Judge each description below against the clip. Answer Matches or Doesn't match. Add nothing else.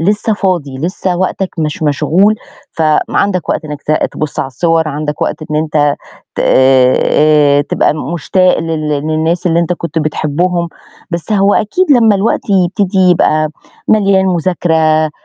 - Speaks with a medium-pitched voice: Matches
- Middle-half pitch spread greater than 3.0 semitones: Matches